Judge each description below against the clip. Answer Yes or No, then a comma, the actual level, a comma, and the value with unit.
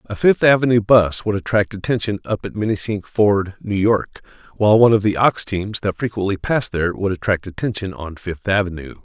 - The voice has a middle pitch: No, low, 100 Hz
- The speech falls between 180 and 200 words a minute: Yes, average, 190 wpm